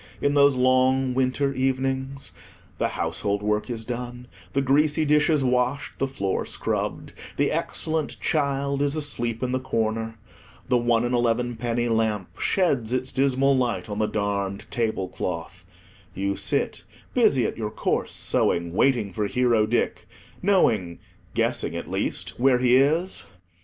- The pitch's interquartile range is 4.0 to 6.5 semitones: No, average, 3.4 semitones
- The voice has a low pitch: Yes, low, 125 Hz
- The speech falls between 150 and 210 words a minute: No, average, 140 wpm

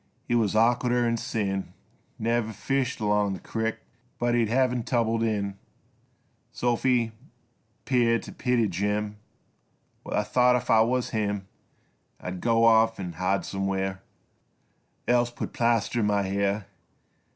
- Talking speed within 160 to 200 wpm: No, average, 140 wpm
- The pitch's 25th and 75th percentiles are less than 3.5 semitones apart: Yes, average, 2.9 semitones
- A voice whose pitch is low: Yes, low, 115 Hz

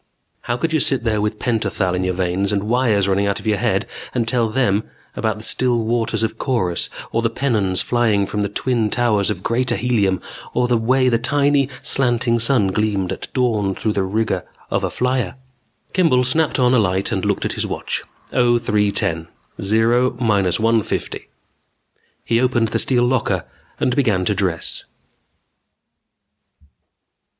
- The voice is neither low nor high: No, low, 115 Hz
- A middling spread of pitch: Yes, average, 3.6 semitones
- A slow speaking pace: No, average, 170 wpm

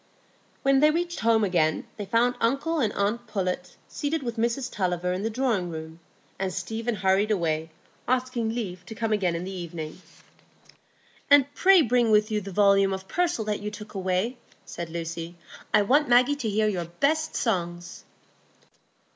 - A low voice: No, high, 210 Hz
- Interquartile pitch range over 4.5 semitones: Yes, average, 5.1 semitones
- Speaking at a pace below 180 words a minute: Yes, average, 170 wpm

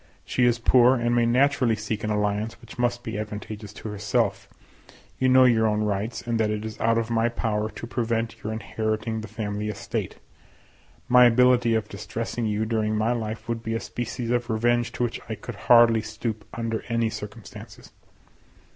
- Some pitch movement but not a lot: No, narrow, 1.8 semitones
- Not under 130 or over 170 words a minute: No, average, 185 wpm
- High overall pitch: No, low, 115 Hz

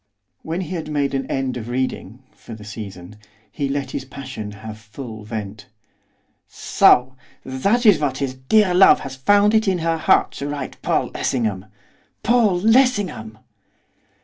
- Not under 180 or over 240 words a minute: No, average, 155 wpm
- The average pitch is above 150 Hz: No, low, 135 Hz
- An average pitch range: No, wide, 8.1 semitones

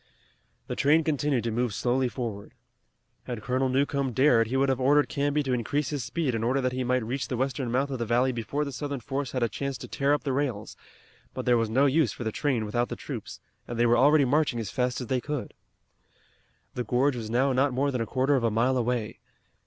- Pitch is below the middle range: Yes, low, 130 Hz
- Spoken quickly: Yes, fast, 240 wpm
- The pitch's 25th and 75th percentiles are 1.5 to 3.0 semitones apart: Yes, average, 2.7 semitones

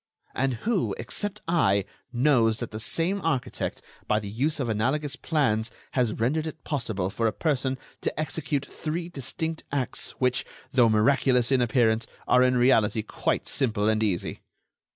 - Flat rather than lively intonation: No, average, 5.2 semitones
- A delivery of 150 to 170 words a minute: Yes, average, 155 wpm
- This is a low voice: Yes, low, 125 Hz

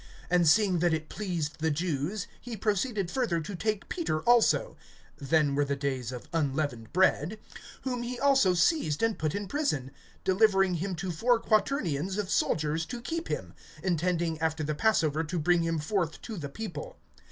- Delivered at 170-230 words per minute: Yes, average, 175 wpm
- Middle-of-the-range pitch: Yes, medium, 175 Hz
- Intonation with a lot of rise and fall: Yes, wide, 5.7 semitones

